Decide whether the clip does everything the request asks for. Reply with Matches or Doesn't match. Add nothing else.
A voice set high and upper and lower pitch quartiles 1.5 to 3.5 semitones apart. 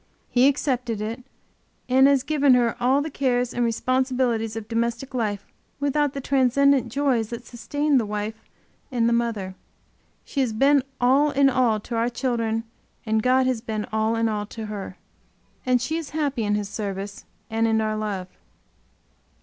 Matches